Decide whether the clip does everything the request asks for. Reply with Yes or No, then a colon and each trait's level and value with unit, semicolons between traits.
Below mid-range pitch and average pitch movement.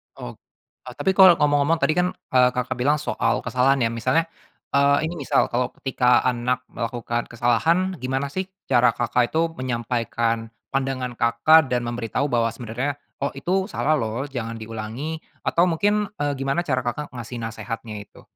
Yes: low, 130 Hz; average, 4.0 semitones